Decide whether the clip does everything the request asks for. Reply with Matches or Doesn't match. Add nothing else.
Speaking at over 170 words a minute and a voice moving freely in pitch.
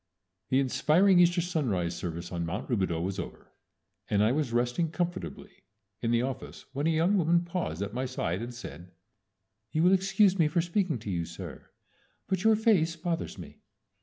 Matches